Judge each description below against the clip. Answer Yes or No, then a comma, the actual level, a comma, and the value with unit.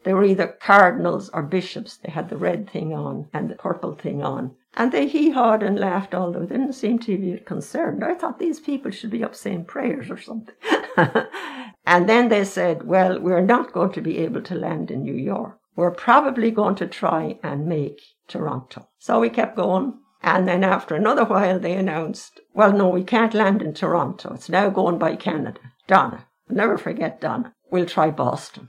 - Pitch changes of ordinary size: Yes, average, 4.4 semitones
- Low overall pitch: No, high, 200 Hz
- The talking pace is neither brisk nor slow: Yes, average, 195 wpm